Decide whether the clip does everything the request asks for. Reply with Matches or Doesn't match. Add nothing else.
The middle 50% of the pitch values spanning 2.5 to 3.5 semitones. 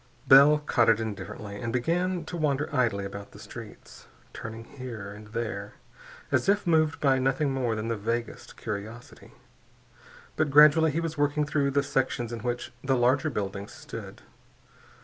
Doesn't match